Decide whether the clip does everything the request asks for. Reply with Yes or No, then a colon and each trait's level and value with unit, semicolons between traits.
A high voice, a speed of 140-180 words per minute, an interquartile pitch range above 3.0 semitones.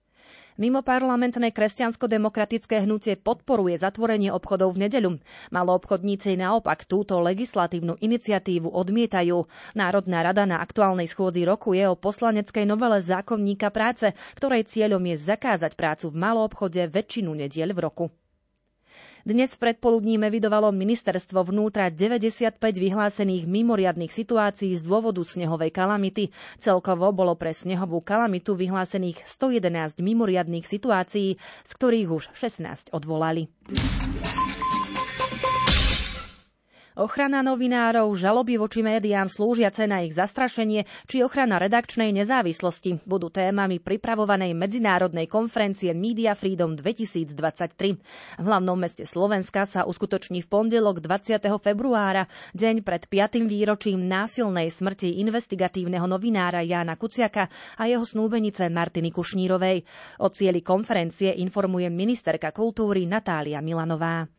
No: high, 200 Hz; average, 115 wpm; average, 3.7 semitones